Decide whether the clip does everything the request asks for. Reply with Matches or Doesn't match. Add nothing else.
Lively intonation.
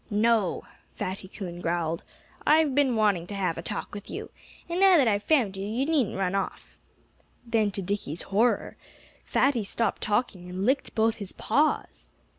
Doesn't match